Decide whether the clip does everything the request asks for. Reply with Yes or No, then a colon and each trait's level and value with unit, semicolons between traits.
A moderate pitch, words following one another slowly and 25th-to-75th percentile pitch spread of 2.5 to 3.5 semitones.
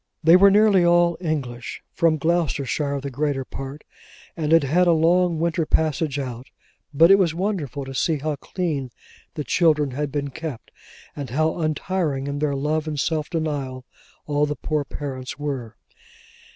No: medium, 150 Hz; average, 165 wpm; average, 3.0 semitones